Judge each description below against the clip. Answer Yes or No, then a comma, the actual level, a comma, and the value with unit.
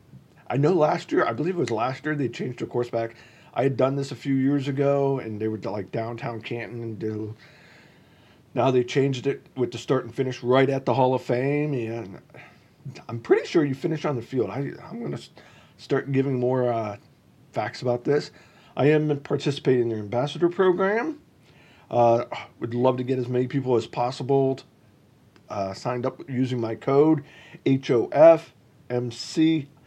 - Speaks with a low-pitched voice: Yes, low, 130 Hz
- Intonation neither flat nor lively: Yes, average, 3.1 semitones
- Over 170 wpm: Yes, average, 190 wpm